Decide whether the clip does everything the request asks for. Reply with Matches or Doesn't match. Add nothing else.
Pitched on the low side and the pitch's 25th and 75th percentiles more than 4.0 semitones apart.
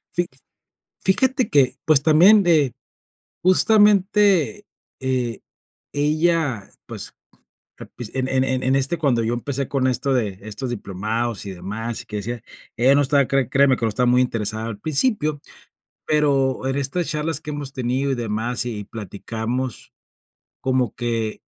Matches